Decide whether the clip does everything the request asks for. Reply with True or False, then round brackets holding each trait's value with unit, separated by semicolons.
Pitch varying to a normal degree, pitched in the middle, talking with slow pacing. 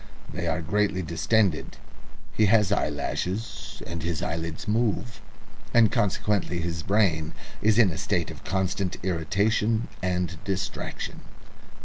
False (3.9 semitones; 95 Hz; 120 wpm)